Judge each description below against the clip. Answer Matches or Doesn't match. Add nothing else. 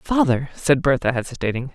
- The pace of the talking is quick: Doesn't match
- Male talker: Doesn't match